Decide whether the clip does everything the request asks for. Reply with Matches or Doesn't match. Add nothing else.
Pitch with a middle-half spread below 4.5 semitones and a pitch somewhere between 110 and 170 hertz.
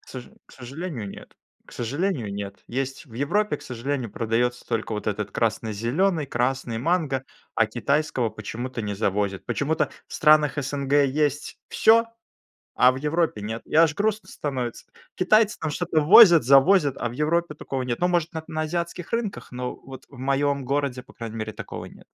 Doesn't match